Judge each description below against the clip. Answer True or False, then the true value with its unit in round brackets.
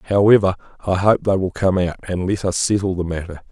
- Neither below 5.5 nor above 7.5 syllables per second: True (5.8 syllables/s)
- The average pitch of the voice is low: True (95 Hz)